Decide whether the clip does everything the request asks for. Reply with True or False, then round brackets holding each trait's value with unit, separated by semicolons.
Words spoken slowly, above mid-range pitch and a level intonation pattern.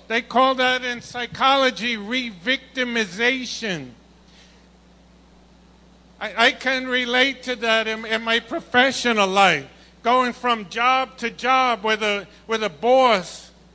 True (120 wpm; 240 Hz; 2.3 semitones)